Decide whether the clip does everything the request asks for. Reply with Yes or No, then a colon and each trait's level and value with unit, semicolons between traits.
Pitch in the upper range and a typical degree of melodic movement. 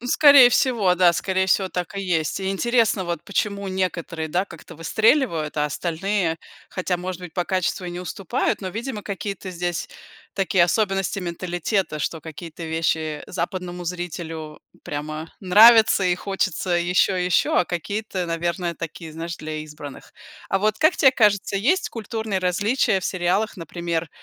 No: medium, 180 Hz; average, 3.0 semitones